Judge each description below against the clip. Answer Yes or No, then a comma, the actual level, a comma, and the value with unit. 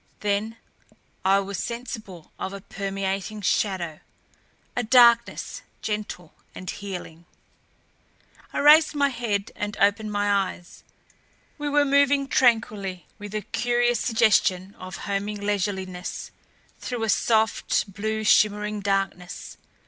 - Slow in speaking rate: Yes, slow, 115 wpm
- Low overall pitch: No, high, 205 Hz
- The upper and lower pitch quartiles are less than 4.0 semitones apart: Yes, average, 2.9 semitones